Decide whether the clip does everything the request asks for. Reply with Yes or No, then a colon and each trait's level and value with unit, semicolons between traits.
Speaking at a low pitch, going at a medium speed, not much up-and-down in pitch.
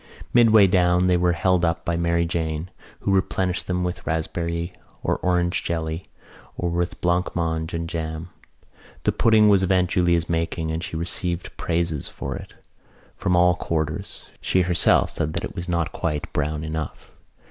Yes: very low, 85 Hz; average, 165 wpm; narrow, 1.6 semitones